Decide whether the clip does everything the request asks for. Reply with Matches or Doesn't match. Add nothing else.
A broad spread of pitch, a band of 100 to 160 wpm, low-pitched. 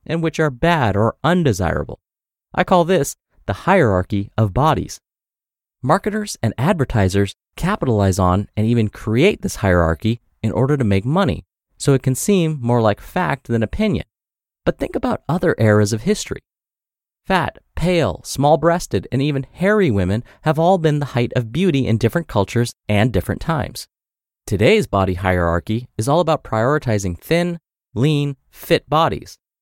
Matches